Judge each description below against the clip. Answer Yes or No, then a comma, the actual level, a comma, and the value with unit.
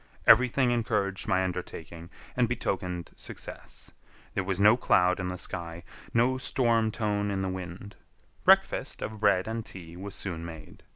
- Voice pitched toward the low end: Yes, very low, 95 Hz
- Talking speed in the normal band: Yes, average, 155 wpm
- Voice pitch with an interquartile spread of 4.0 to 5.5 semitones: No, average, 3.5 semitones